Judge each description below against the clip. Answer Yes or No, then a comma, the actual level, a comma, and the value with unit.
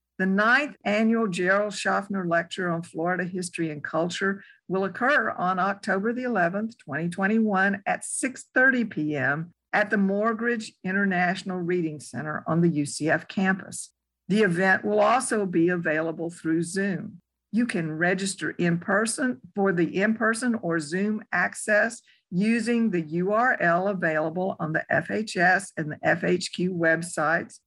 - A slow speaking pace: Yes, slow, 130 wpm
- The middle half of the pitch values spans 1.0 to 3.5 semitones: No, average, 3.9 semitones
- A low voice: No, high, 190 Hz